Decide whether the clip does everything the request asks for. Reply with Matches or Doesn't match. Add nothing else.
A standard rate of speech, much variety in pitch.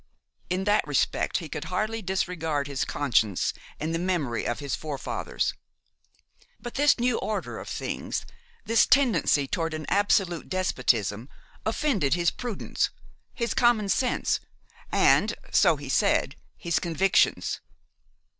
Doesn't match